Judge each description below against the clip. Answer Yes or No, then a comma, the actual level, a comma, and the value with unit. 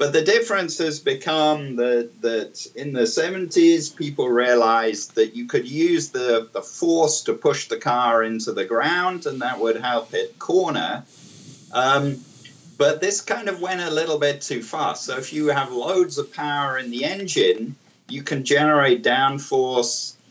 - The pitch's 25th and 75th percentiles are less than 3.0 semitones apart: No, wide, 5.6 semitones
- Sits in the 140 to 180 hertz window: Yes, medium, 150 Hz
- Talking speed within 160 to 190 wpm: Yes, average, 170 wpm